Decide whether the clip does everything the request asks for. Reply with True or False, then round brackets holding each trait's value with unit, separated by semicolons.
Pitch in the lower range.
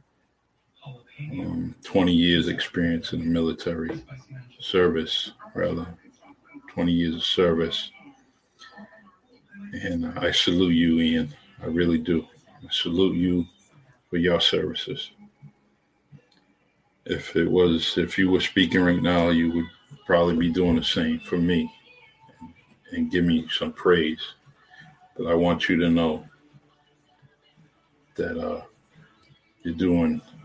True (90 Hz)